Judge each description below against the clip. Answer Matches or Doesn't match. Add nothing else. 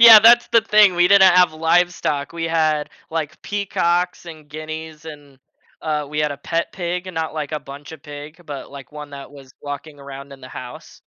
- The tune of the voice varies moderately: Matches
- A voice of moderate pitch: Matches